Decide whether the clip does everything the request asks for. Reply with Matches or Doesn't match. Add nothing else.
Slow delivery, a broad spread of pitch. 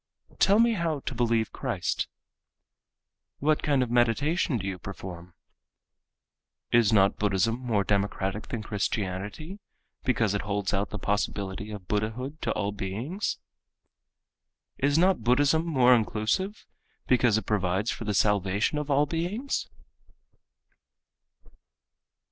Matches